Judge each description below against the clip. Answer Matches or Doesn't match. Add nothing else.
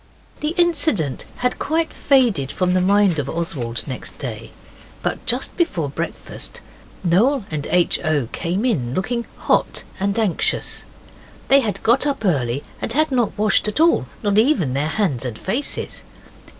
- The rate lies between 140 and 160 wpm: Matches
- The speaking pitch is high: Matches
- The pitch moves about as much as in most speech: Doesn't match